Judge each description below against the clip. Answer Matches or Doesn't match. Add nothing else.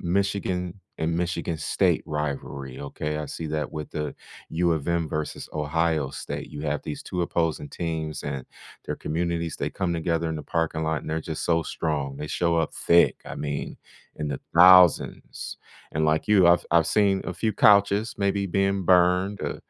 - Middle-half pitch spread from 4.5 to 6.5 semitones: Doesn't match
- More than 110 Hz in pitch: Doesn't match